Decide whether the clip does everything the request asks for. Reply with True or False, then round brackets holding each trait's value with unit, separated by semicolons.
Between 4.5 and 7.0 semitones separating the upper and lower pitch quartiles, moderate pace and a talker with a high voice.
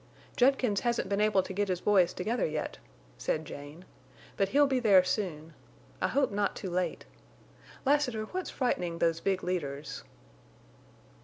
True (5.5 semitones; 150 wpm; 195 Hz)